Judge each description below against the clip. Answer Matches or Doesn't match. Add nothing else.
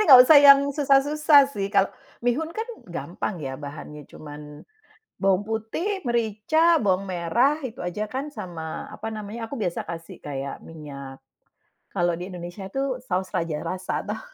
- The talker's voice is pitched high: Matches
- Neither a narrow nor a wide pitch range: Doesn't match